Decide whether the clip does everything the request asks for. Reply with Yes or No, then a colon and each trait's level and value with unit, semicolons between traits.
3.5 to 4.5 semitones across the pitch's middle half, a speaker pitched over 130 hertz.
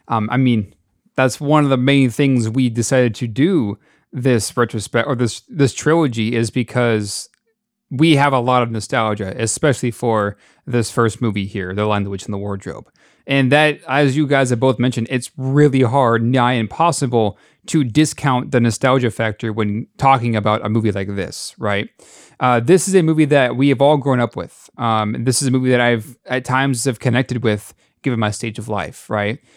No: average, 3.8 semitones; low, 125 Hz